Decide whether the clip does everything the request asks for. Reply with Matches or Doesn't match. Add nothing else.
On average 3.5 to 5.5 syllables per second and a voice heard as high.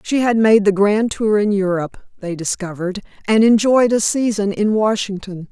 Matches